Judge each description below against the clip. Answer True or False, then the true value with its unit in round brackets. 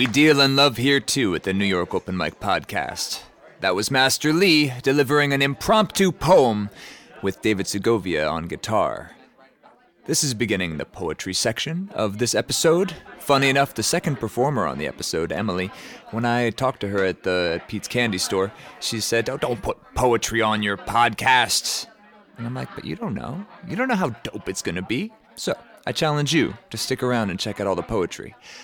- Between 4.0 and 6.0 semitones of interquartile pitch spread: True (5.6 semitones)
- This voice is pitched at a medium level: False (120 Hz)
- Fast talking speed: False (195 wpm)